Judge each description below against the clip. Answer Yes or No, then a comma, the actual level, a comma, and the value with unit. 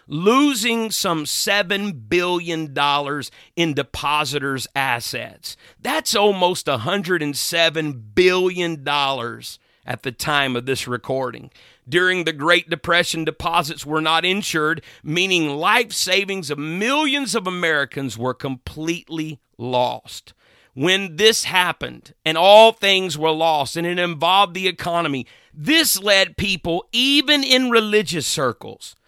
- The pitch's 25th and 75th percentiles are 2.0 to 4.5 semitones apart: No, average, 5.0 semitones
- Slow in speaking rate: Yes, slow, 115 wpm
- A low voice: No, medium, 170 Hz